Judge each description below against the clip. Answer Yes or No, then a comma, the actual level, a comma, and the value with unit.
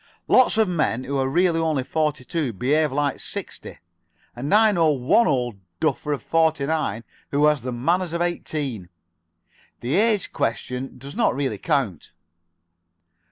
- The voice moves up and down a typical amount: Yes, average, 4.3 semitones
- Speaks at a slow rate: No, average, 155 wpm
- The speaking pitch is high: No, medium, 145 Hz